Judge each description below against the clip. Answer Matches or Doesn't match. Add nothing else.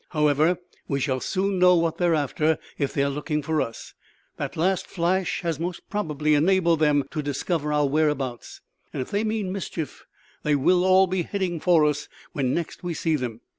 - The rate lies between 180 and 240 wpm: Matches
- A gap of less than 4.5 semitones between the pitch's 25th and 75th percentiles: Matches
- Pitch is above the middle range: Doesn't match